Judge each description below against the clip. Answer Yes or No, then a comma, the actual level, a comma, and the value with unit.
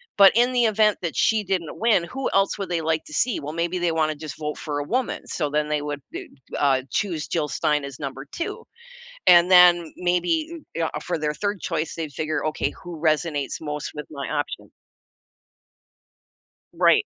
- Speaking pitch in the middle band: Yes, medium, 165 Hz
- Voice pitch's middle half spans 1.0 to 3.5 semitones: No, average, 4.0 semitones